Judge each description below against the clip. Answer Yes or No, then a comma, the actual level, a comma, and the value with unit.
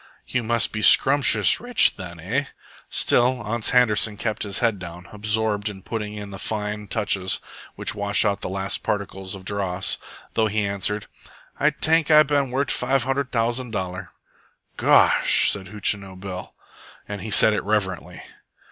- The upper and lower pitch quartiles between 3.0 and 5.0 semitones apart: Yes, average, 3.3 semitones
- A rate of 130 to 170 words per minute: Yes, average, 160 wpm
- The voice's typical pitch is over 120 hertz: No, low, 105 Hz